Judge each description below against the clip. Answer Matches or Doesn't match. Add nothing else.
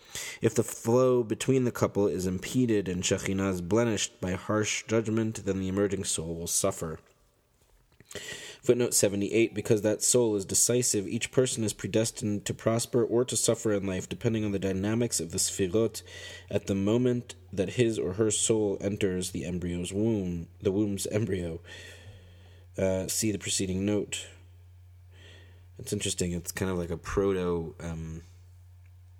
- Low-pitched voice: Matches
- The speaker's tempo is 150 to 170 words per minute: Matches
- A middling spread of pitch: Matches